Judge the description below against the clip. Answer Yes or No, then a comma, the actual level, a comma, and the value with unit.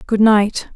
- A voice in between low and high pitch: No, high, 210 Hz